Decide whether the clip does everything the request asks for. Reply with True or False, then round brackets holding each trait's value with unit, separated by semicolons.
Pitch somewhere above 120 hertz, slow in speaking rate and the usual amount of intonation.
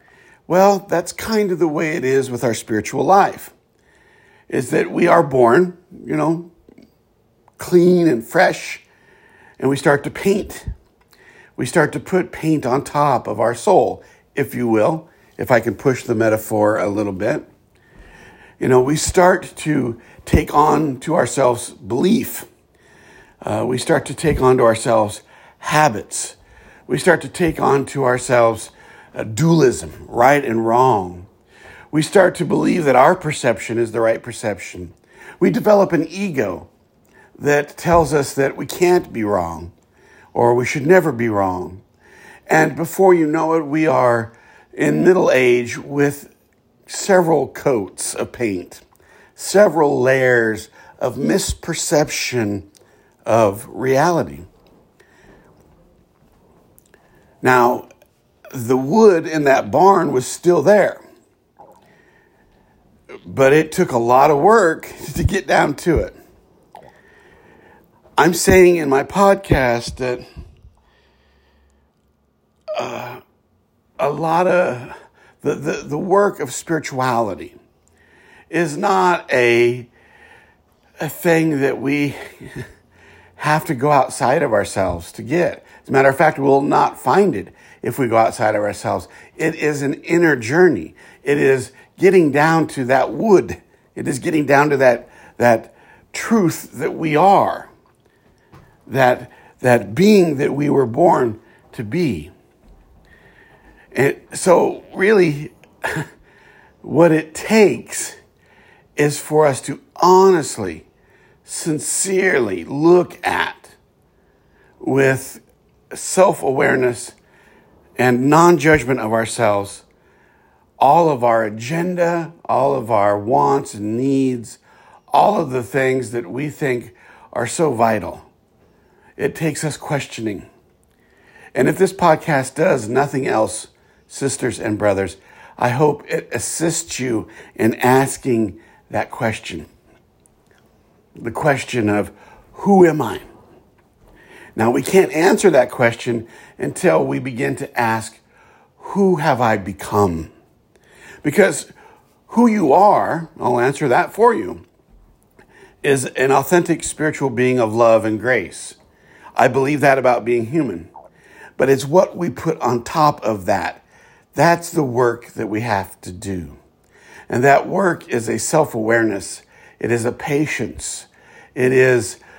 False (135 Hz; 130 wpm; 5.9 semitones)